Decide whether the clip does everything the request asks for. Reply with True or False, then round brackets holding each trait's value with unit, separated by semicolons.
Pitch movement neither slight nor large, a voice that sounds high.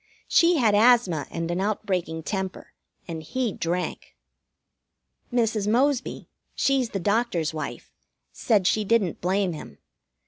True (5.0 semitones; 205 Hz)